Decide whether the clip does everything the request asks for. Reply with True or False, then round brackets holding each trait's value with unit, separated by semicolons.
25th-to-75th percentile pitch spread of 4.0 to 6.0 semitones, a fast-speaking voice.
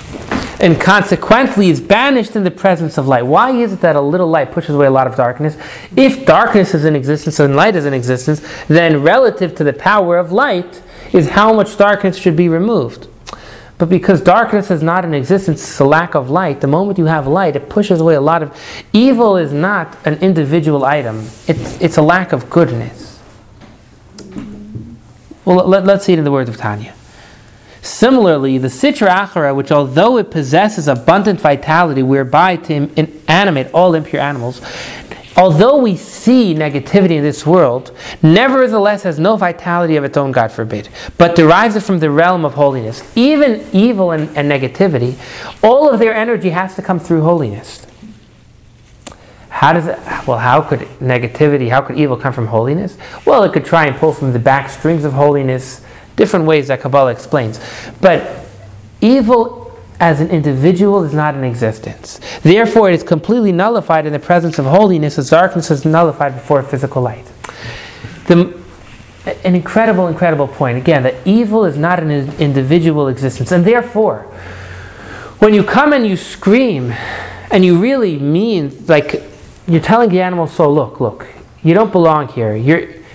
False (5.4 semitones; 175 wpm)